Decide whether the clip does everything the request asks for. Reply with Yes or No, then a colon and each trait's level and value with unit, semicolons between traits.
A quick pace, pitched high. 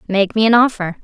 Yes: fast, 235 wpm; high, 210 Hz